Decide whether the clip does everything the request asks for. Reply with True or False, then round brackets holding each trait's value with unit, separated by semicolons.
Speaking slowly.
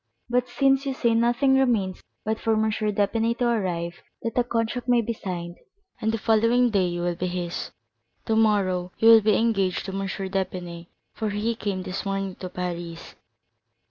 False (175 wpm)